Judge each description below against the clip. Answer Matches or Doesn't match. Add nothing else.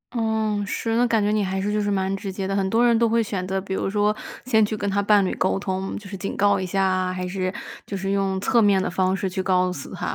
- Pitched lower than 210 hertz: Matches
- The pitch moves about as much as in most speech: Doesn't match